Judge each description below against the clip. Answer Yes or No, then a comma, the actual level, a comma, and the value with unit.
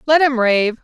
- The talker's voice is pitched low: No, very high, 250 Hz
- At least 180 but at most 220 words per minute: Yes, fast, 215 wpm